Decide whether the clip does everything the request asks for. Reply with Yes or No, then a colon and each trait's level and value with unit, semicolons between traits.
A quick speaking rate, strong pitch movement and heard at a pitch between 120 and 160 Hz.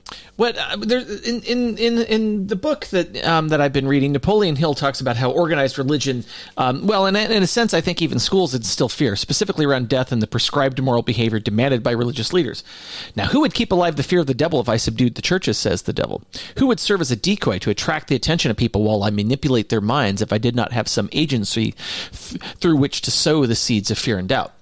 Yes: fast, 235 wpm; wide, 7.4 semitones; medium, 140 Hz